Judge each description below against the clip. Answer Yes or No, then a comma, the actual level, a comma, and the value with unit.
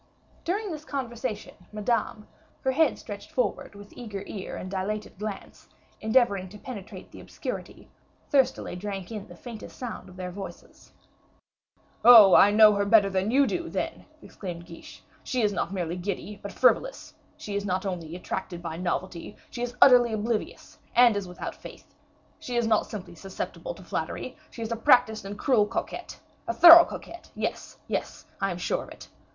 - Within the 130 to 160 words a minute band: No, average, 175 wpm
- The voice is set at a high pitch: Yes, high, 210 Hz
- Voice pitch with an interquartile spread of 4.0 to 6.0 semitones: Yes, average, 4.3 semitones